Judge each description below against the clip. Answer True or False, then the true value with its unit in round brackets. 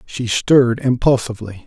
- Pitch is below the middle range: True (115 Hz)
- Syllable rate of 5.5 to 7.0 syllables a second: False (5.1 syllables/s)